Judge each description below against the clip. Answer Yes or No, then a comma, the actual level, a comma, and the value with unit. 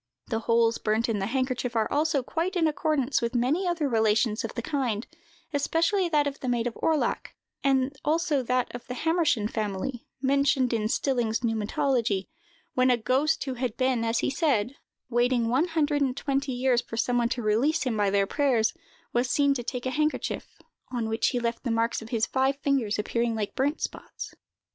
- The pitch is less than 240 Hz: No, very high, 250 Hz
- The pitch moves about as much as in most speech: Yes, average, 3.6 semitones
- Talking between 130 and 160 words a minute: No, average, 195 wpm